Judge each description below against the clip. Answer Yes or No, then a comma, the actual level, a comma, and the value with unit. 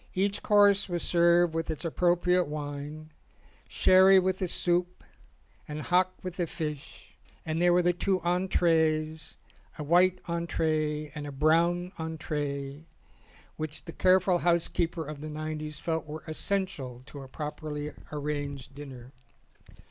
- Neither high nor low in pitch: Yes, medium, 160 Hz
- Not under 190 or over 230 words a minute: No, average, 140 wpm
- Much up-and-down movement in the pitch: No, average, 2.8 semitones